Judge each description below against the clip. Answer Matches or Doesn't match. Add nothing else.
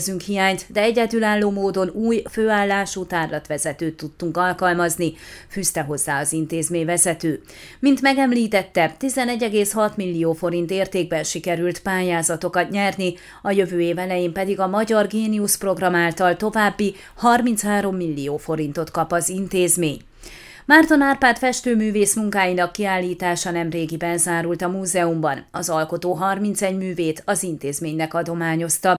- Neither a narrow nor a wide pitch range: Matches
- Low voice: Doesn't match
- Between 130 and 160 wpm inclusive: Doesn't match